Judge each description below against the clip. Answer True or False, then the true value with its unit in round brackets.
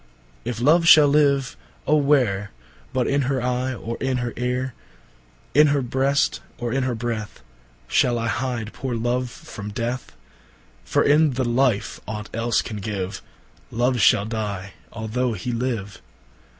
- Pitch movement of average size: True (3.8 semitones)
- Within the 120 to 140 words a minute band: True (135 wpm)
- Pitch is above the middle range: False (120 Hz)